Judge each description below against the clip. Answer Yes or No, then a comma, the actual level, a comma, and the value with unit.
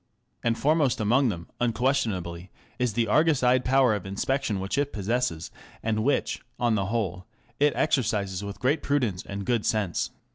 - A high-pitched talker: No, low, 115 Hz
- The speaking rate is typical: Yes, average, 160 wpm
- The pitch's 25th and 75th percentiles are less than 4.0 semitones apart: No, average, 4.7 semitones